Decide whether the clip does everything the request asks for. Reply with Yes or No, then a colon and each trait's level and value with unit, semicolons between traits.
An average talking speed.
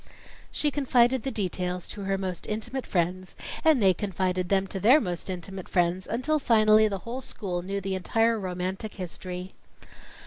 Yes: average, 165 wpm